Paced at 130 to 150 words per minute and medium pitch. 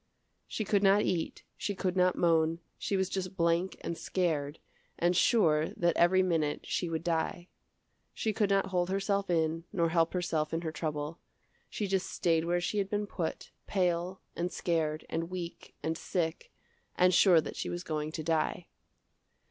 No: average, 175 wpm; medium, 175 Hz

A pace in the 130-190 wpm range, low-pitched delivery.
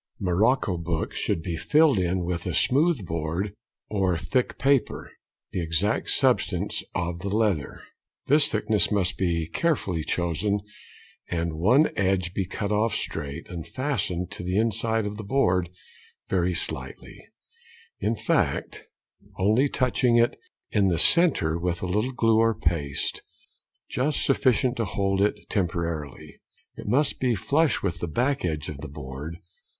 Yes: average, 150 wpm; very low, 95 Hz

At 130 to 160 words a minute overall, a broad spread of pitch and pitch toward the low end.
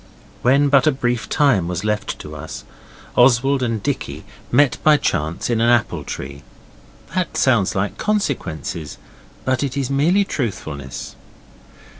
Yes: average, 140 wpm; wide, 6.3 semitones; low, 125 Hz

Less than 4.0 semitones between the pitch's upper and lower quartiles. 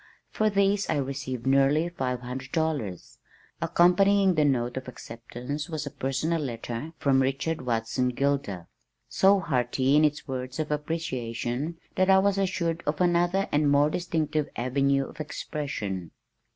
No: average, 4.6 semitones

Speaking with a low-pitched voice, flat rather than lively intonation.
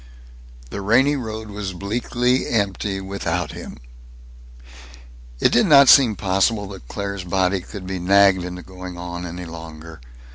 No: very low, 95 Hz; average, 3.1 semitones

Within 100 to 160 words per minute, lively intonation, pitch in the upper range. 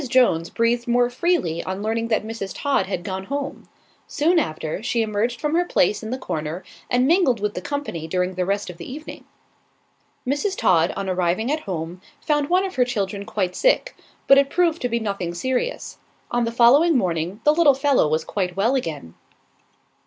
No: average, 190 wpm; wide, 7.2 semitones; high, 230 Hz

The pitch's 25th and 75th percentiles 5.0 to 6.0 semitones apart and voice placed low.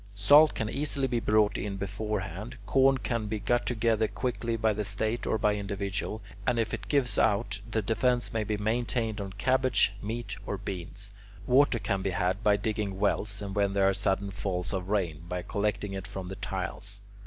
No: average, 2.8 semitones; low, 105 Hz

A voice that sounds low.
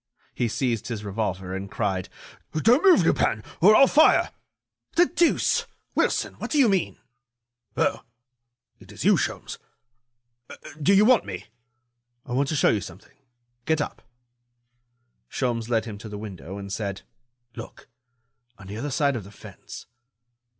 Yes: low, 115 Hz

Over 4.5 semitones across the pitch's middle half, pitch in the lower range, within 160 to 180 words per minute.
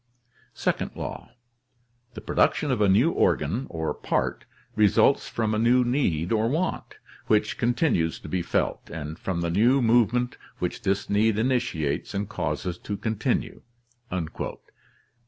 No: average, 5.2 semitones; low, 110 Hz; average, 145 wpm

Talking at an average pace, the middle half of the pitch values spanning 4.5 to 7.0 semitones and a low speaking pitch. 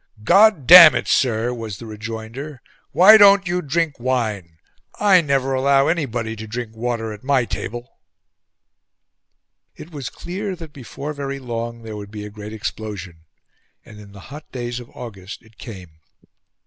Yes: average, 160 wpm; average, 4.9 semitones; low, 120 Hz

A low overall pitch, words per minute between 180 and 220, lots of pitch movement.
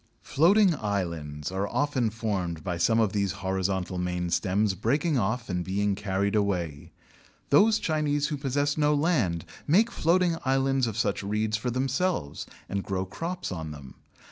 No: low, 105 Hz; average, 155 wpm; wide, 7.5 semitones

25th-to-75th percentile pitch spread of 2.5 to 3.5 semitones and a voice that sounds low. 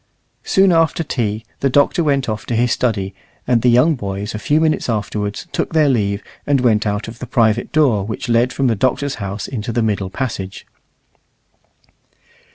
No: average, 4.6 semitones; low, 120 Hz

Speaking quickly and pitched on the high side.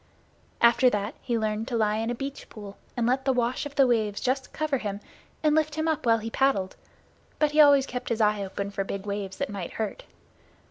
Yes: fast, 225 wpm; high, 235 Hz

